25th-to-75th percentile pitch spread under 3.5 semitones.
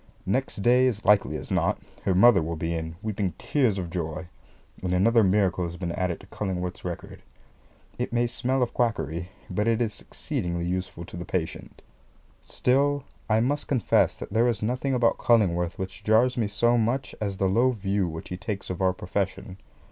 No: average, 4.7 semitones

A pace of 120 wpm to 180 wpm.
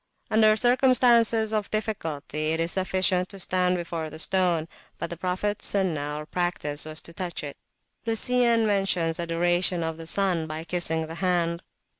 Yes: average, 160 wpm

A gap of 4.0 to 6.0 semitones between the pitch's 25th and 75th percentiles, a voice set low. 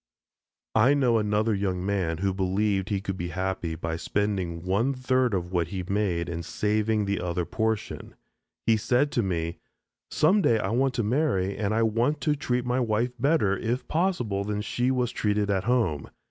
Yes: average, 4.5 semitones; low, 105 Hz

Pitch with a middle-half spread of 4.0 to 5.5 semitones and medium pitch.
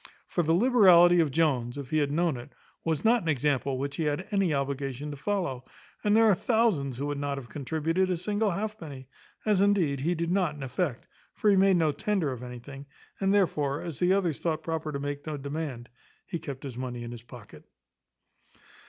Yes: average, 4.8 semitones; medium, 155 Hz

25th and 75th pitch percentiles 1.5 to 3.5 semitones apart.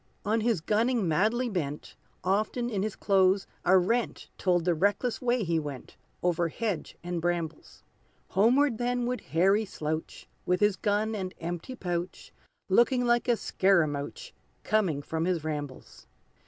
No: average, 5.1 semitones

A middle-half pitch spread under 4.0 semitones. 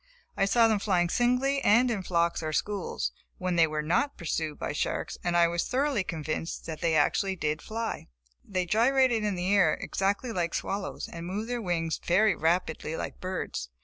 No: average, 4.7 semitones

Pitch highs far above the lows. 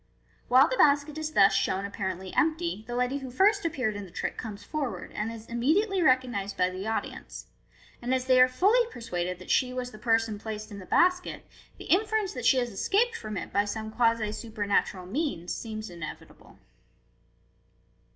Yes: wide, 5.9 semitones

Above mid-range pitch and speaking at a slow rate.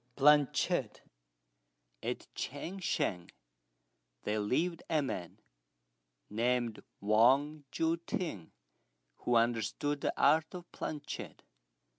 No: medium, 140 Hz; slow, 90 wpm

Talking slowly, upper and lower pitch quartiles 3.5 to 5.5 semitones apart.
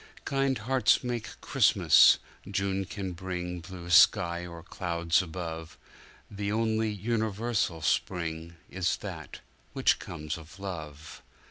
Yes: slow, 105 wpm; average, 4.0 semitones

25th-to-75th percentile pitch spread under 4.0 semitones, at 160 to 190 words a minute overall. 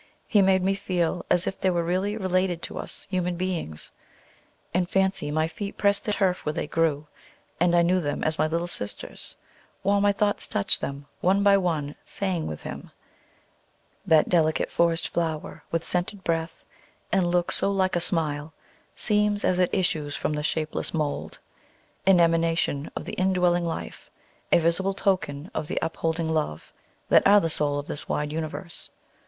Yes: average, 3.2 semitones; average, 175 wpm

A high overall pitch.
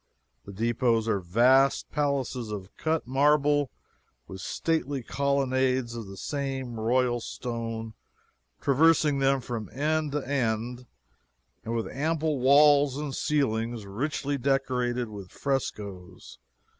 No: low, 130 Hz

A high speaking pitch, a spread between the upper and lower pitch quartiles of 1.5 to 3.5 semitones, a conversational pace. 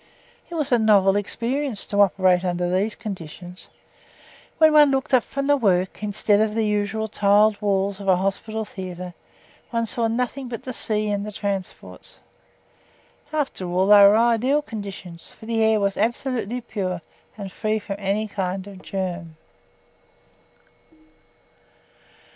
Yes: high, 210 Hz; average, 3.1 semitones; average, 150 wpm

